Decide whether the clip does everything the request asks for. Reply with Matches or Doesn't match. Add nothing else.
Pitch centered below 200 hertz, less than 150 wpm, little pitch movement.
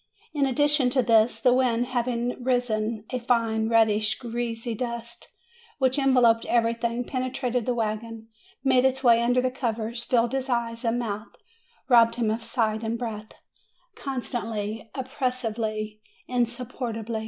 Doesn't match